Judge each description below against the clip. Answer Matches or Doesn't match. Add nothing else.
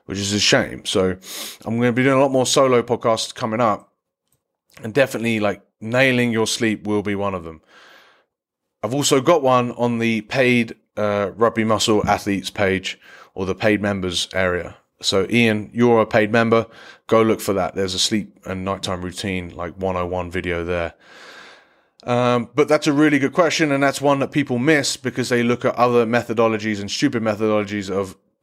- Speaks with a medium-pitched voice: Doesn't match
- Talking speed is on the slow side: Doesn't match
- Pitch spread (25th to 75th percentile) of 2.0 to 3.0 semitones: Doesn't match